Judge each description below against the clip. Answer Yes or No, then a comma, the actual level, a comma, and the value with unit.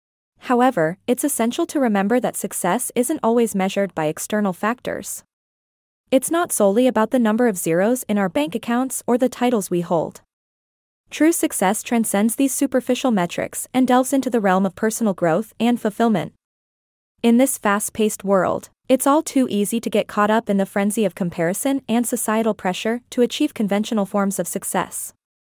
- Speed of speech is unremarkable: Yes, average, 170 wpm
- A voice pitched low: No, high, 225 Hz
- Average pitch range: Yes, average, 4.0 semitones